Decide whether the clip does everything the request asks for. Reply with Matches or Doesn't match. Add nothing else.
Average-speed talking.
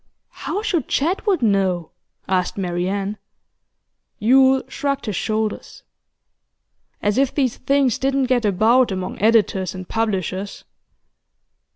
Doesn't match